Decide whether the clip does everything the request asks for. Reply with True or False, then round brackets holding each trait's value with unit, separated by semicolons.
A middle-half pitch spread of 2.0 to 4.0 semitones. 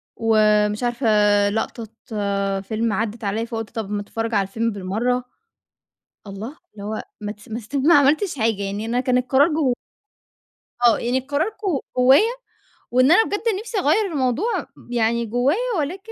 False (4.5 semitones)